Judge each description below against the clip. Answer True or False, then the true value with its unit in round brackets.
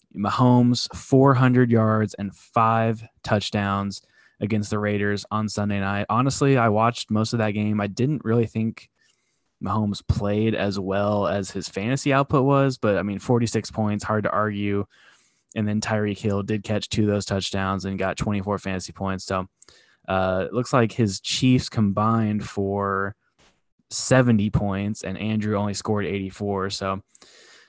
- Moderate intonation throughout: False (2.2 semitones)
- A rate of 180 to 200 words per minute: False (155 wpm)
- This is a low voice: True (105 Hz)